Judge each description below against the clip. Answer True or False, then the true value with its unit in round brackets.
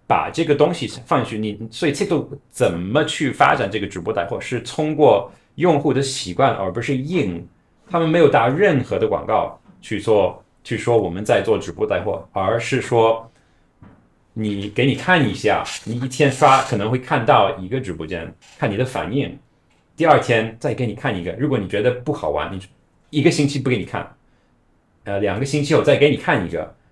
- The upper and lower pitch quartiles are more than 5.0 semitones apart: True (5.4 semitones)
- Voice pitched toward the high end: False (130 Hz)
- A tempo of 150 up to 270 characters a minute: False (285 characters per minute)